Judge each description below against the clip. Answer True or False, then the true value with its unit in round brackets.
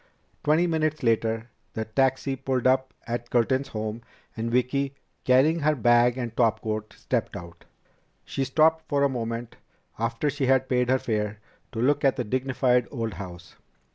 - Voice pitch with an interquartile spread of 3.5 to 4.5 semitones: False (3.0 semitones)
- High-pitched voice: False (125 Hz)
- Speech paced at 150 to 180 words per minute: True (165 wpm)